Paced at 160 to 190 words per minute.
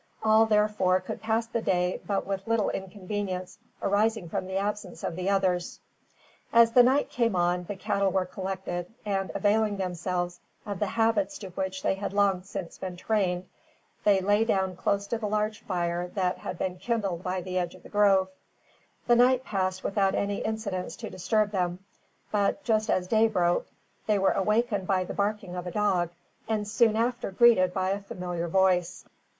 Yes: average, 180 wpm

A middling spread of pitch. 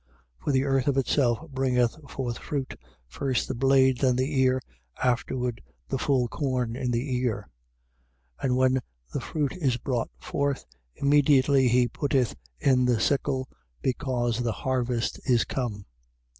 No: narrow, 1.8 semitones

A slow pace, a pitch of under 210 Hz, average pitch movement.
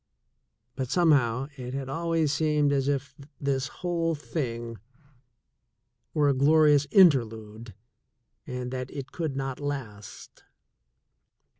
Yes: slow, 110 wpm; medium, 140 Hz; average, 3.1 semitones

